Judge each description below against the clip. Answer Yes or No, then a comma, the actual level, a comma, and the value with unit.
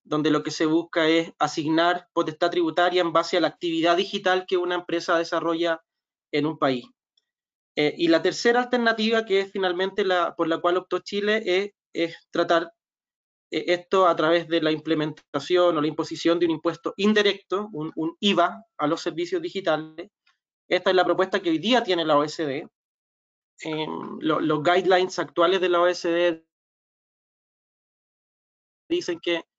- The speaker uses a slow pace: No, average, 160 wpm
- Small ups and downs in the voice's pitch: Yes, narrow, 2.2 semitones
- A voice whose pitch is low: No, medium, 175 Hz